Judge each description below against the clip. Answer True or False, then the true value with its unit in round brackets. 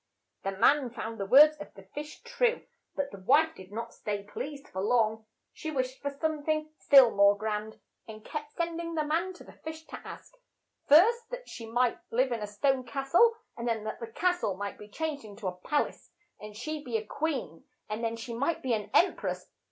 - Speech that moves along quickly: True (225 wpm)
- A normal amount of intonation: False (6.2 semitones)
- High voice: True (255 Hz)